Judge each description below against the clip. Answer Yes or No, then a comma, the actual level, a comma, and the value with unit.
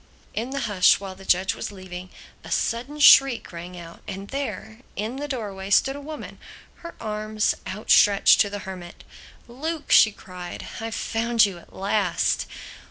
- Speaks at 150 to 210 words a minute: Yes, average, 165 wpm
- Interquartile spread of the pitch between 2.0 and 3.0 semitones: No, average, 4.2 semitones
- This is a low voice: No, high, 210 Hz